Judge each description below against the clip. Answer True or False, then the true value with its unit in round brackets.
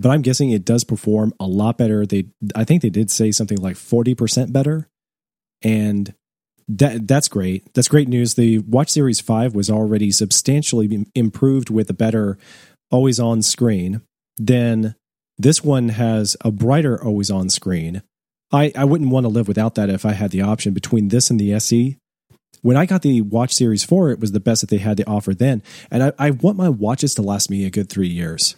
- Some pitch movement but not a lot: True (3.6 semitones)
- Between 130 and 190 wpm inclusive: False (205 wpm)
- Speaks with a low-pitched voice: True (115 Hz)